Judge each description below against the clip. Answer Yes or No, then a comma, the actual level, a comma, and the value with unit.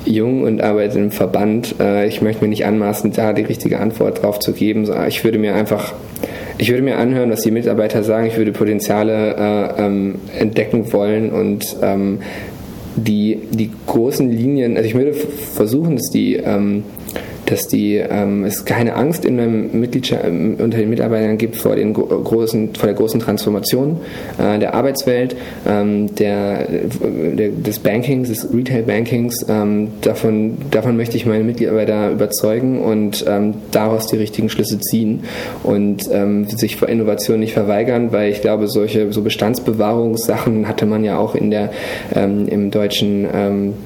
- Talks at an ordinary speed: Yes, average, 155 wpm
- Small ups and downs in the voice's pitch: Yes, narrow, 1.6 semitones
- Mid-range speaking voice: No, low, 110 Hz